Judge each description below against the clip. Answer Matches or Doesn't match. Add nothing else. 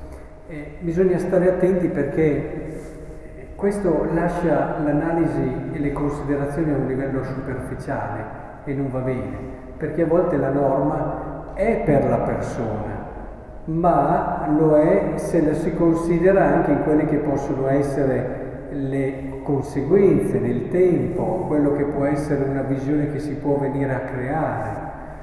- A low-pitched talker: Doesn't match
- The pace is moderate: Matches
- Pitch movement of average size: Matches